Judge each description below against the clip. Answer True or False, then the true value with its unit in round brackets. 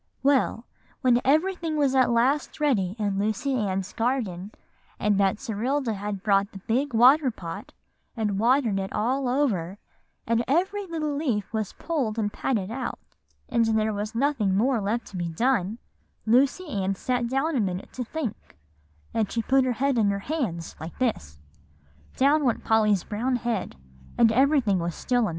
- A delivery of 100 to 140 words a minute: False (165 wpm)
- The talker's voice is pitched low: False (230 Hz)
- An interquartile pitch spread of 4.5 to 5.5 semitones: True (4.9 semitones)